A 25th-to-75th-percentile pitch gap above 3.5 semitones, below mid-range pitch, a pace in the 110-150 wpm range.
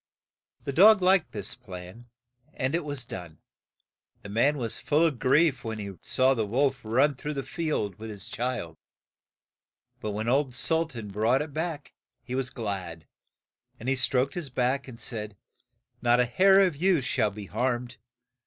No: average, 5.1 semitones; low, 125 Hz; average, 170 wpm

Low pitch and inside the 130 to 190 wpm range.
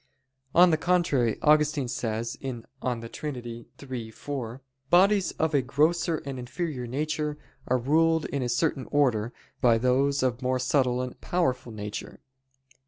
Yes: low, 130 Hz; average, 145 wpm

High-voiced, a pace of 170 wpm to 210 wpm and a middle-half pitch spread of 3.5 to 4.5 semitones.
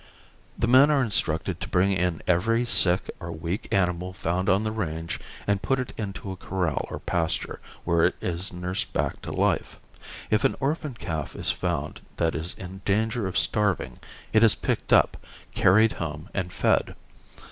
No: very low, 95 Hz; average, 175 wpm; average, 4.1 semitones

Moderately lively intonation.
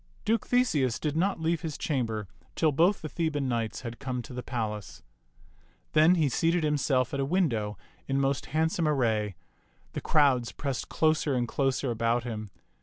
Yes: average, 5.0 semitones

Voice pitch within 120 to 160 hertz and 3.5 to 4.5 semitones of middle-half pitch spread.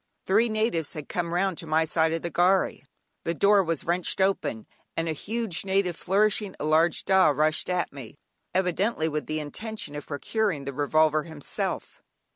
No: medium, 170 Hz; average, 3.9 semitones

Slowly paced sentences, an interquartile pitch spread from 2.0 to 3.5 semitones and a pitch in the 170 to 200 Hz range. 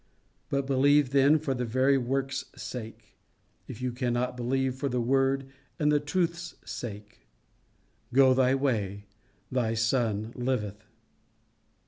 No: slow, 125 wpm; narrow, 2.4 semitones; low, 130 Hz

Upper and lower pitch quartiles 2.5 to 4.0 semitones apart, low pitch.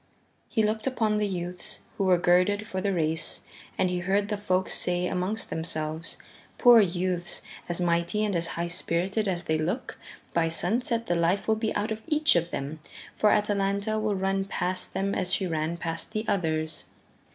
No: average, 3.5 semitones; medium, 185 Hz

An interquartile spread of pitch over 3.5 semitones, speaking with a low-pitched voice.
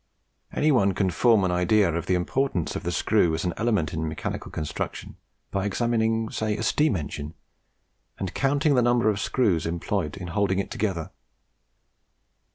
Yes: average, 4.9 semitones; low, 100 Hz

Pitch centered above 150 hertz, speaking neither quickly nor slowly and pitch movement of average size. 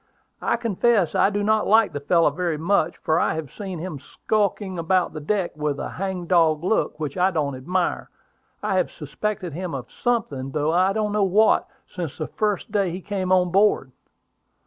Yes: medium, 185 Hz; average, 195 wpm; average, 4.5 semitones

